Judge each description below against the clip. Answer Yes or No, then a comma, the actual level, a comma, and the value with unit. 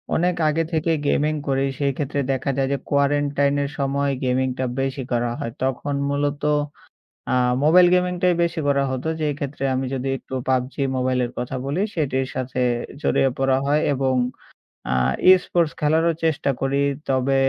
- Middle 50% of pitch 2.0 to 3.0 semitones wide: Yes, narrow, 2.4 semitones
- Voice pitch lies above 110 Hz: Yes, medium, 140 Hz